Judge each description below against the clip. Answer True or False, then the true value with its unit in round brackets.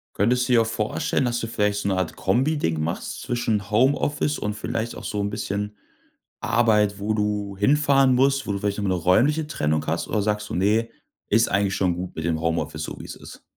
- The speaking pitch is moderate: False (105 Hz)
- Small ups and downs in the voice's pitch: False (3.4 semitones)